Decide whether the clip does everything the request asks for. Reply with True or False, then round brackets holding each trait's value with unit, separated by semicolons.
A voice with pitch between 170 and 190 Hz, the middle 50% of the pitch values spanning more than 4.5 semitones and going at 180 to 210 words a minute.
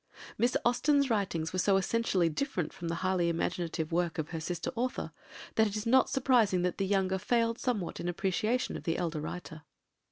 True (185 Hz; 5.3 semitones; 190 wpm)